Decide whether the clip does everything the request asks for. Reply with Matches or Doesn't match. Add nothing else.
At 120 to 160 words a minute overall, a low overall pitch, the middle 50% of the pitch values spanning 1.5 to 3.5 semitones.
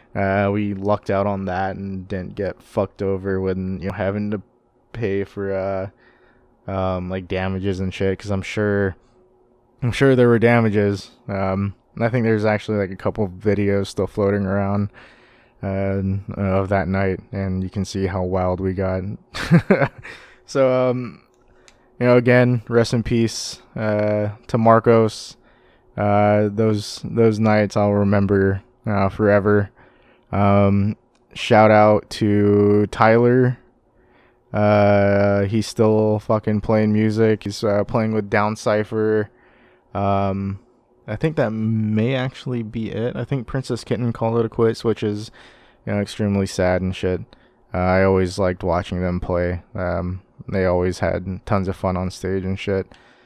Matches